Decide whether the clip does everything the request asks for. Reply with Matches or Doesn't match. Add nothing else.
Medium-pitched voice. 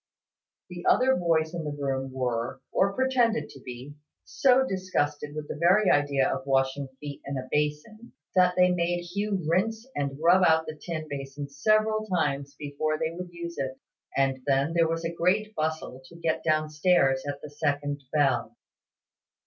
Matches